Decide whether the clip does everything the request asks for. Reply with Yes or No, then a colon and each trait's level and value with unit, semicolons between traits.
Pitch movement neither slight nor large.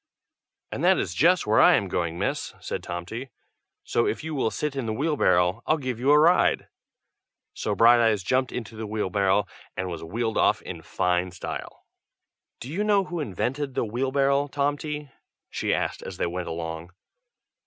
No: wide, 7.5 semitones